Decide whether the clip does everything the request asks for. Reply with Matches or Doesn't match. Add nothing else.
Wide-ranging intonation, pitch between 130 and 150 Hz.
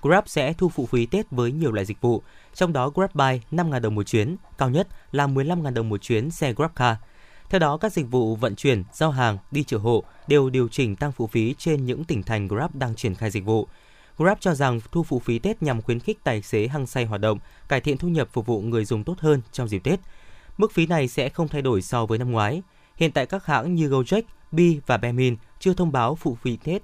Matches